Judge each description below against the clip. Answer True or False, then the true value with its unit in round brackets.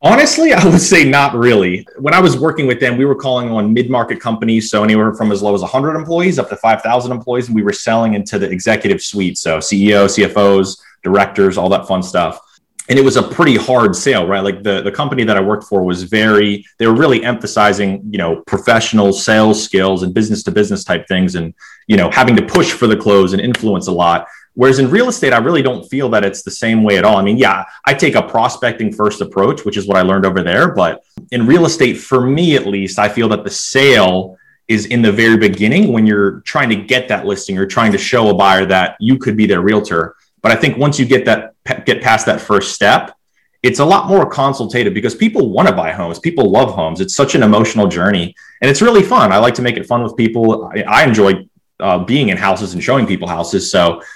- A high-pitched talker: False (110 Hz)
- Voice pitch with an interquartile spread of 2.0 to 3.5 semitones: False (4.0 semitones)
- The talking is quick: True (235 wpm)